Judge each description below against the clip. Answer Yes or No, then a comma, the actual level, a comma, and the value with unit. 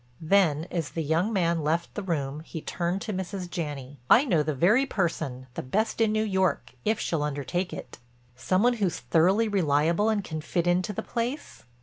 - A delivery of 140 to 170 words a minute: No, average, 195 wpm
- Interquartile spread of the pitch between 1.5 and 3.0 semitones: No, average, 5.0 semitones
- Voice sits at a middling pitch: Yes, medium, 175 Hz